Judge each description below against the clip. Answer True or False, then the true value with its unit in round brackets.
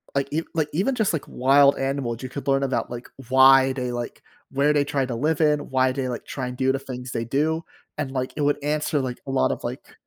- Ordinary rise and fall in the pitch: False (2.2 semitones)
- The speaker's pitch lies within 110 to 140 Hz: True (135 Hz)